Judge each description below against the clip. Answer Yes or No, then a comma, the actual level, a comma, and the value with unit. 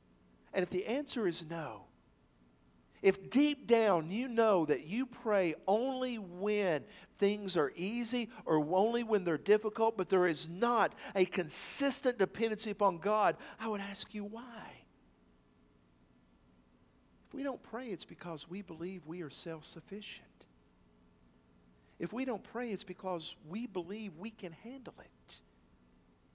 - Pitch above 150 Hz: Yes, high, 190 Hz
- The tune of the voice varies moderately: No, wide, 6.3 semitones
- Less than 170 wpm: Yes, average, 140 wpm